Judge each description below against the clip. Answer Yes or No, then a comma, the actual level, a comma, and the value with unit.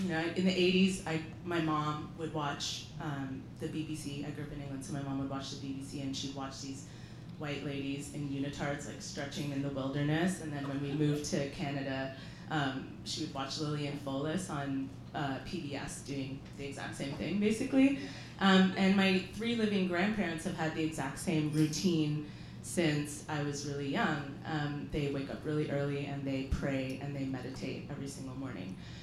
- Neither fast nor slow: Yes, average, 190 wpm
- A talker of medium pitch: Yes, medium, 145 Hz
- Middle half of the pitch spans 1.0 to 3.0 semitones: Yes, average, 2.7 semitones